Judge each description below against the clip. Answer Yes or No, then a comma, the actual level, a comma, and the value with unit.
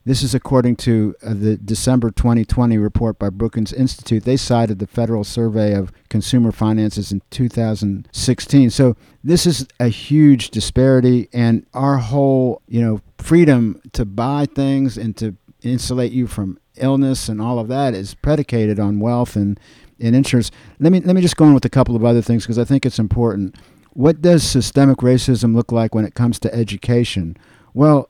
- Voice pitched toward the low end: Yes, low, 120 Hz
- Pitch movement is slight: No, average, 3.2 semitones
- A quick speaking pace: No, average, 175 wpm